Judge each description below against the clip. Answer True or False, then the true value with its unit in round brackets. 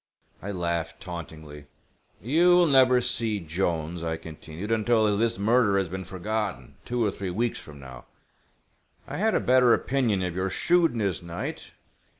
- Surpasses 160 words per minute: False (155 wpm)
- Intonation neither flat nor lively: False (6.0 semitones)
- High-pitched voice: False (100 Hz)